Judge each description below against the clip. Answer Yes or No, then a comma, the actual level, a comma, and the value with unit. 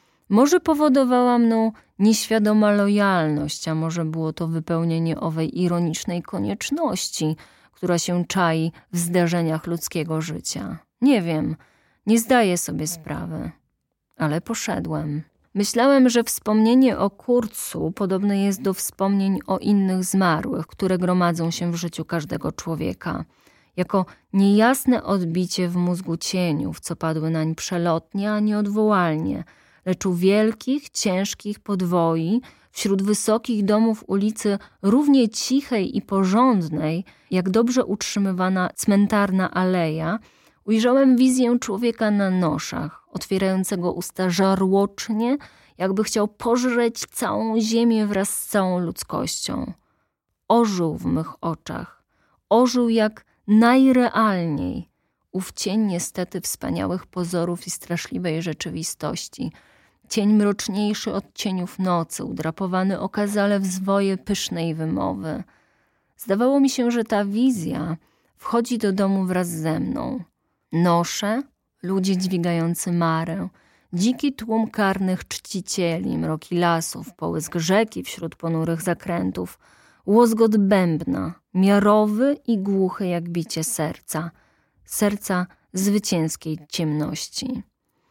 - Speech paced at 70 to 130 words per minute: Yes, slow, 110 wpm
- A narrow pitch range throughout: No, average, 4.2 semitones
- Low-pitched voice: No, high, 190 Hz